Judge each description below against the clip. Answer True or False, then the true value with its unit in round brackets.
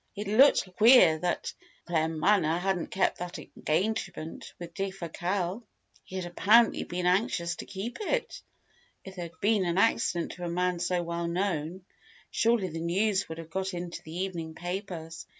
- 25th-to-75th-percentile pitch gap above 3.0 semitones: False (2.6 semitones)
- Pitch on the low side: False (180 Hz)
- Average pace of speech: True (160 wpm)